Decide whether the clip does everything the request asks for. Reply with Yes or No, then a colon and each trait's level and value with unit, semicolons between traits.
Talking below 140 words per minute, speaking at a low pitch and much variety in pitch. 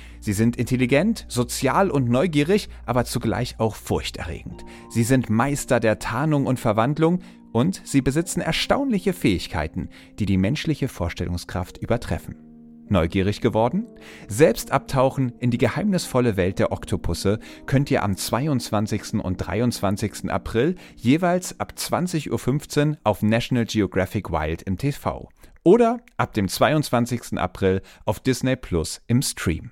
Yes: average, 130 wpm; low, 115 Hz; wide, 6.1 semitones